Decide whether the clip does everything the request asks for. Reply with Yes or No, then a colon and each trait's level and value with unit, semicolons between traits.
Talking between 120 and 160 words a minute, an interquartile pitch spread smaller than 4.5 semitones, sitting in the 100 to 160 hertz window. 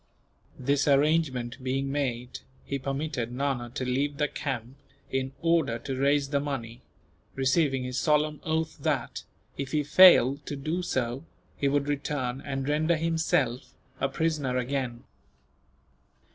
Yes: slow, 135 wpm; narrow, 2.5 semitones; medium, 140 Hz